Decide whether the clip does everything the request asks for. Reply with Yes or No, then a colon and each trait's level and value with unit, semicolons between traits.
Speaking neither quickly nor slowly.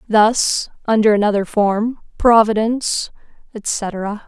No: slow, 85 wpm